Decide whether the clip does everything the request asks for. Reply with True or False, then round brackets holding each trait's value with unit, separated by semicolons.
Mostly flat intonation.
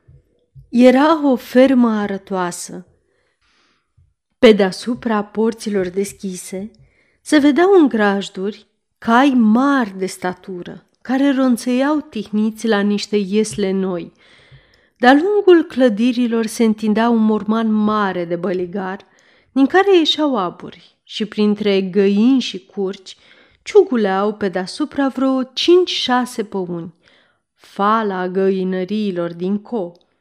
False (4.8 semitones)